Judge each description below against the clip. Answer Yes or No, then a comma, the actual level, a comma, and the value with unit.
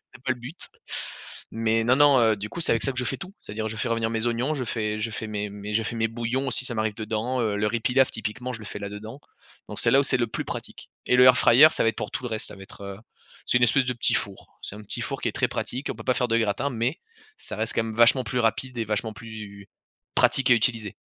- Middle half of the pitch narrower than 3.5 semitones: Yes, average, 2.8 semitones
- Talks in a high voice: No, low, 115 Hz